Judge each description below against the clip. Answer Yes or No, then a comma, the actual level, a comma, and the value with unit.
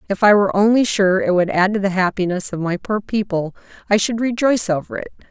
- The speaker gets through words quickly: Yes, fast, 225 wpm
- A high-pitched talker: Yes, high, 200 Hz